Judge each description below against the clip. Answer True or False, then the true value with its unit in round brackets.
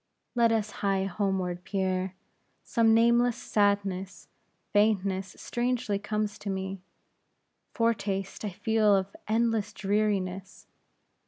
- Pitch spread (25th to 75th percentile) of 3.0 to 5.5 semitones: False (2.5 semitones)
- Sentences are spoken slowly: True (100 wpm)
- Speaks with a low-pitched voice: False (205 Hz)